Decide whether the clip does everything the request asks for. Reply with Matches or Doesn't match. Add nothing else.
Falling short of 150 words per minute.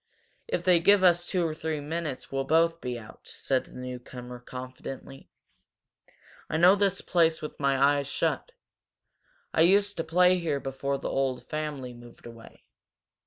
Doesn't match